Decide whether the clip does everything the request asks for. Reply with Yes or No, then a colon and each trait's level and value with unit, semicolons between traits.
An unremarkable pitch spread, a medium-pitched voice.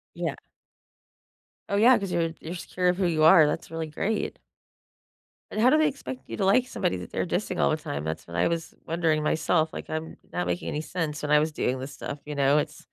Yes: average, 3.6 semitones; medium, 160 Hz